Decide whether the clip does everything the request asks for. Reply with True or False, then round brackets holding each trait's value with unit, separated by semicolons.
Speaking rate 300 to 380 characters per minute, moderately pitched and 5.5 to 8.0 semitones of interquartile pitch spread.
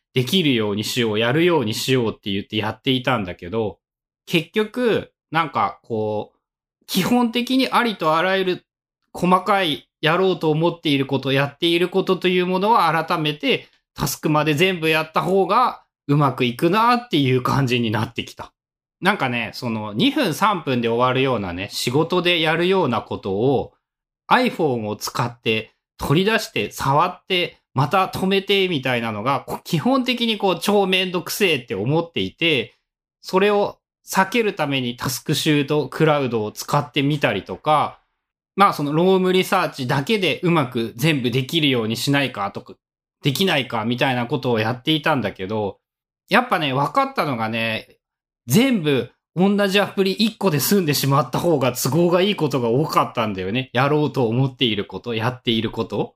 True (350 characters per minute; 145 Hz; 7.3 semitones)